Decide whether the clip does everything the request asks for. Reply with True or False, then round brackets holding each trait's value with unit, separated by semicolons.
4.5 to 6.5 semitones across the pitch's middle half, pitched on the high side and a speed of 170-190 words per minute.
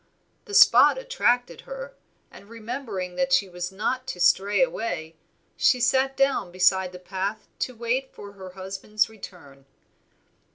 False (5.6 semitones; 210 Hz; 140 wpm)